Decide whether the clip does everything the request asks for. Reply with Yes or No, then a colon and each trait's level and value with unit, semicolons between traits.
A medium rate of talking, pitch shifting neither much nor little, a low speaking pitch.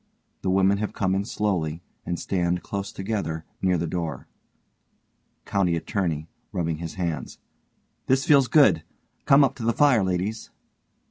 Yes: average, 145 wpm; average, 3.9 semitones; very low, 95 Hz